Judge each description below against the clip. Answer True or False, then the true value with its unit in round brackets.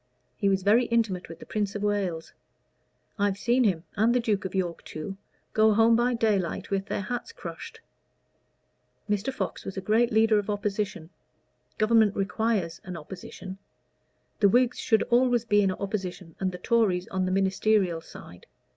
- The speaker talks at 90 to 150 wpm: False (165 wpm)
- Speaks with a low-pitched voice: False (205 Hz)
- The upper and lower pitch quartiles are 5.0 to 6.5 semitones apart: False (2.9 semitones)